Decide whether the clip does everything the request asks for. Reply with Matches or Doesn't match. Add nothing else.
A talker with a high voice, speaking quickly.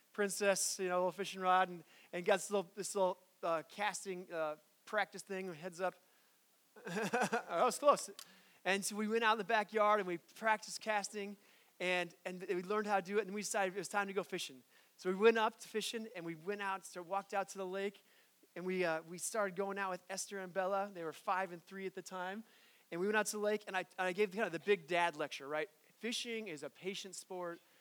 Matches